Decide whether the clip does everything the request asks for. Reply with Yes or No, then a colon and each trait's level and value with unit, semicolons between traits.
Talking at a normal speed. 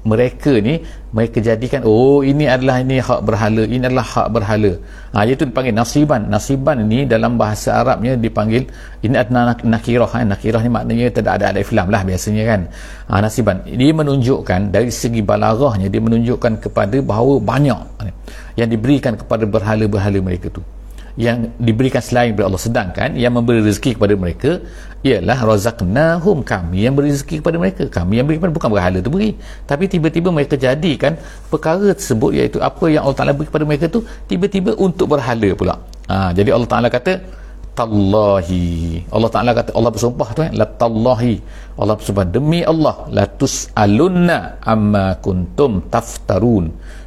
Yes: average, 160 wpm